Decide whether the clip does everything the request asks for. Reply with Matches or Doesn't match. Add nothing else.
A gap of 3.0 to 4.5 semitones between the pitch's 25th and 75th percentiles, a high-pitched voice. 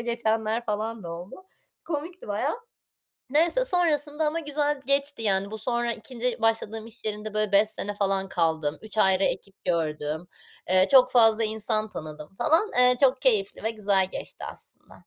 Doesn't match